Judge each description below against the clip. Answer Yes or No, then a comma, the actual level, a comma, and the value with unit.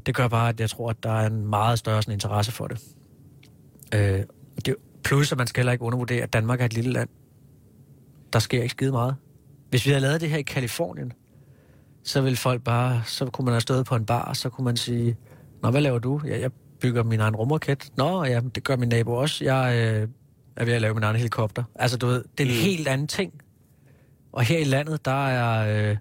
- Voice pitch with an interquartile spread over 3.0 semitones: No, average, 2.7 semitones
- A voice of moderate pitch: No, low, 125 Hz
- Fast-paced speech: Yes, fast, 235 wpm